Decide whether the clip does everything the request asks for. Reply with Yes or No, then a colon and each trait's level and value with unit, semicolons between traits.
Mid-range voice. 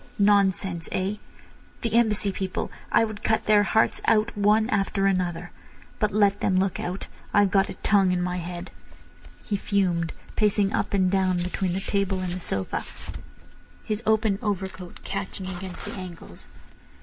No: high, 195 Hz